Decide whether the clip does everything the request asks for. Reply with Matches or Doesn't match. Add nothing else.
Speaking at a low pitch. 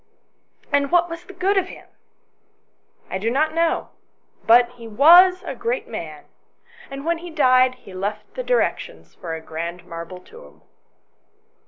Doesn't match